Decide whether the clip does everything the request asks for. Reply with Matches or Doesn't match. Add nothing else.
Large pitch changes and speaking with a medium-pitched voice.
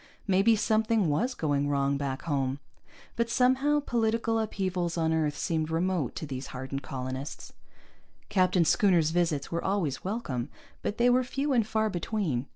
Matches